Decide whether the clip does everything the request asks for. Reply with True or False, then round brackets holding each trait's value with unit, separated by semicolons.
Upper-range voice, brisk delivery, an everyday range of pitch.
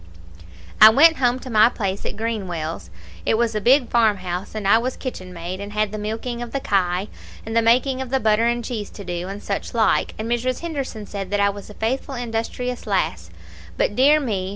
True (220 Hz; 210 wpm; 3.6 semitones)